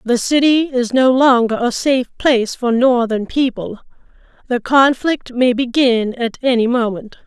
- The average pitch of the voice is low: No, high, 245 Hz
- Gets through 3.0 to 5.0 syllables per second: Yes, 4.5 syllables/s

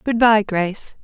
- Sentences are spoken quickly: No, average, 175 wpm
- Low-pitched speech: No, high, 210 Hz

